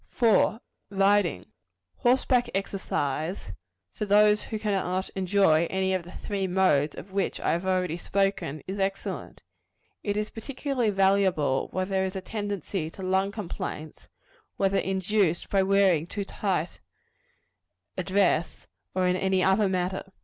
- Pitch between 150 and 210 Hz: Yes, high, 190 Hz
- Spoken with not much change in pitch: Yes, narrow, 1.9 semitones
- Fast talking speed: No, average, 140 wpm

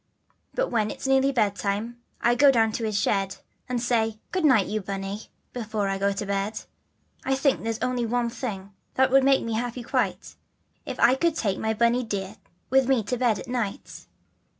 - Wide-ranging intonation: No, average, 3.6 semitones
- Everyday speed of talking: Yes, average, 195 wpm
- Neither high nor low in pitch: No, high, 230 Hz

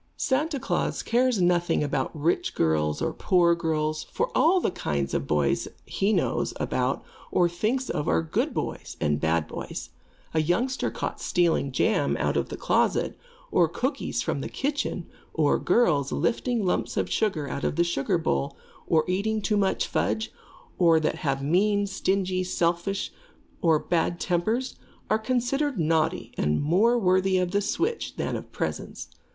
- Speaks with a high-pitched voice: No, medium, 175 Hz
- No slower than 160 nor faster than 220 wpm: Yes, average, 165 wpm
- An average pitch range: No, wide, 5.9 semitones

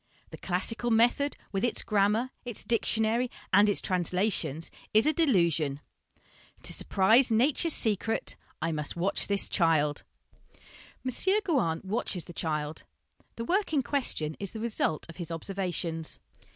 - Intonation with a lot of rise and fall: Yes, wide, 6.0 semitones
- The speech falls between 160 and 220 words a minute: No, average, 140 wpm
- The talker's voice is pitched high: Yes, high, 200 Hz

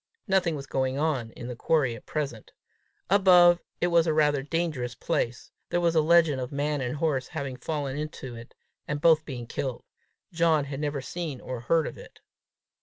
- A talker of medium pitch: Yes, medium, 150 Hz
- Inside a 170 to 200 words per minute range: Yes, average, 185 wpm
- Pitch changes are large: No, average, 3.8 semitones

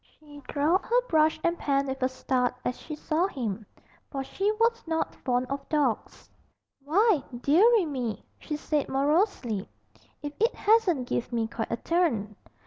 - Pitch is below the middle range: No, very high, 290 Hz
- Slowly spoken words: No, average, 160 wpm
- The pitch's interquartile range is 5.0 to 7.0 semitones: Yes, wide, 5.4 semitones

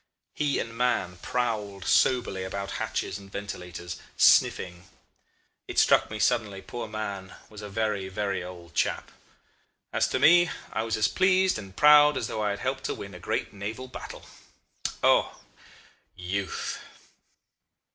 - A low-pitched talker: Yes, low, 105 Hz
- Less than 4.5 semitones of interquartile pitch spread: Yes, average, 4.1 semitones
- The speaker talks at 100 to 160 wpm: Yes, average, 145 wpm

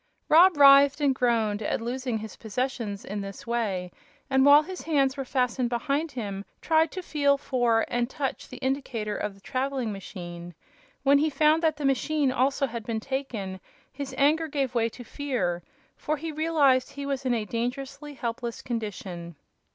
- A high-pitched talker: Yes, very high, 260 Hz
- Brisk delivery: No, average, 175 wpm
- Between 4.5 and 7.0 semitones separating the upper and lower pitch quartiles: No, average, 4.0 semitones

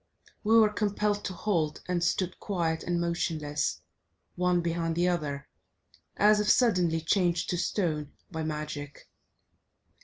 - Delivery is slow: Yes, slow, 130 wpm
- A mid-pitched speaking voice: Yes, medium, 175 Hz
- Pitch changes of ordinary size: Yes, average, 3.6 semitones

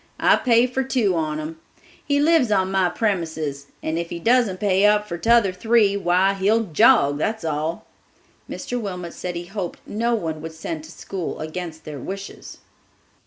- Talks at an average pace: Yes, average, 175 wpm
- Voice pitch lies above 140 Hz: Yes, medium, 185 Hz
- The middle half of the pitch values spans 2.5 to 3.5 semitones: No, average, 5.0 semitones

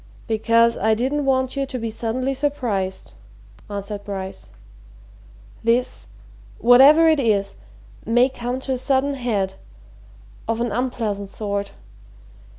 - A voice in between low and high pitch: No, high, 235 Hz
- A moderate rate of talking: No, slow, 120 wpm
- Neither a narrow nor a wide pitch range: Yes, average, 4.0 semitones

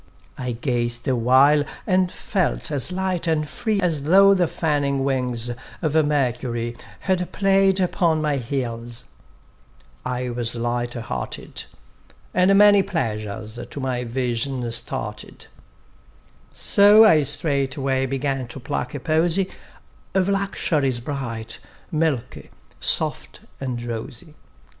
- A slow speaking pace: Yes, slow, 115 wpm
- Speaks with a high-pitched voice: No, medium, 140 Hz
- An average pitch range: No, wide, 6.0 semitones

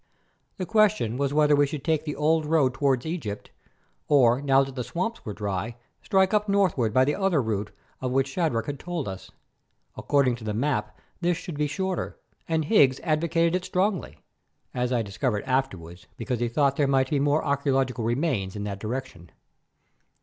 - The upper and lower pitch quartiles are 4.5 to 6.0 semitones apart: Yes, average, 5.3 semitones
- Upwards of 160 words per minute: Yes, average, 180 wpm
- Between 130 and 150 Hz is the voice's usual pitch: Yes, medium, 140 Hz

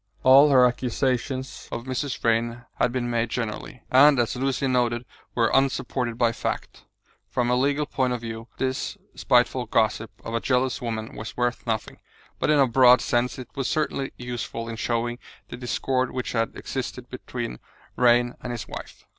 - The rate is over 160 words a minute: Yes, average, 170 wpm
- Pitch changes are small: Yes, narrow, 1.8 semitones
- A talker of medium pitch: No, low, 125 Hz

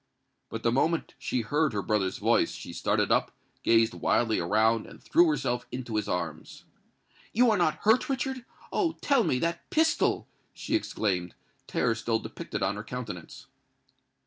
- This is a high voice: No, low, 120 Hz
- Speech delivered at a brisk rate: No, average, 155 wpm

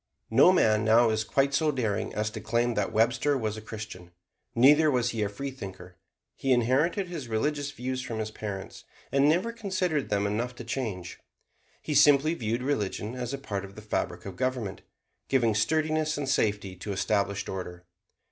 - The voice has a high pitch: No, low, 120 Hz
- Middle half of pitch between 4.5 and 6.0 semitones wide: Yes, average, 4.8 semitones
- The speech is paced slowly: No, average, 175 wpm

